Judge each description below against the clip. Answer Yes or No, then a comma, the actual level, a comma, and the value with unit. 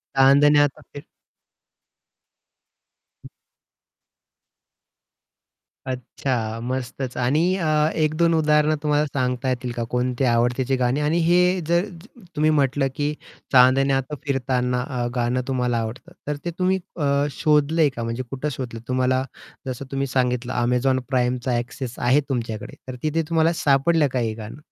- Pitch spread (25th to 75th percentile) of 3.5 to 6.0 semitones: No, average, 3.1 semitones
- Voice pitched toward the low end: Yes, low, 130 Hz